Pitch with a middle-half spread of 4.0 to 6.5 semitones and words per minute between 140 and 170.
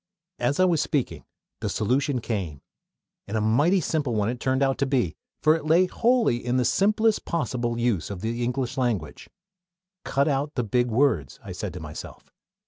No: average, 4.6 semitones; average, 185 wpm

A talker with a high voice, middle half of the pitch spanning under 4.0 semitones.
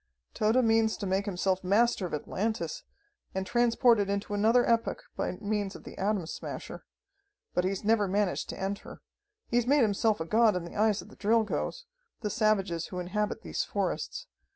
Yes: high, 210 Hz; average, 2.8 semitones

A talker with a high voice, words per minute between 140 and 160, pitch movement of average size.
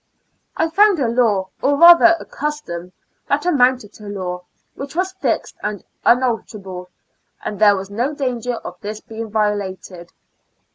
No: high, 225 Hz; average, 145 wpm; wide, 6.1 semitones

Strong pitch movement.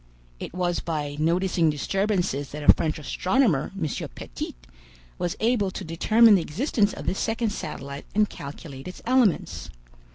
Yes: wide, 5.7 semitones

